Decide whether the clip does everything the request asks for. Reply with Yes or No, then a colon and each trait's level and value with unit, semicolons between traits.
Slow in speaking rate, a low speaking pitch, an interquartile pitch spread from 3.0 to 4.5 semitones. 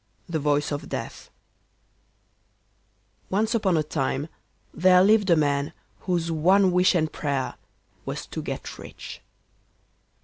No: slow, 125 wpm; medium, 170 Hz; average, 4.1 semitones